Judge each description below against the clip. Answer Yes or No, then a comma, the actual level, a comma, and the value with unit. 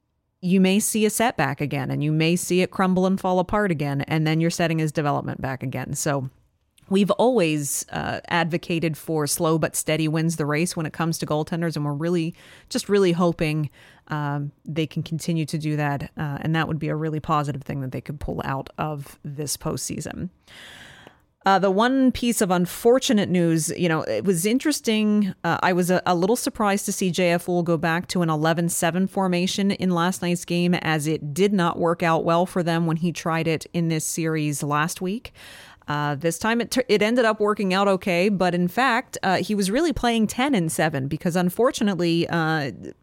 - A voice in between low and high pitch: Yes, medium, 170 Hz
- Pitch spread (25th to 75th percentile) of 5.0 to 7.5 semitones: No, average, 3.6 semitones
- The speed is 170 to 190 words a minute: No, fast, 205 wpm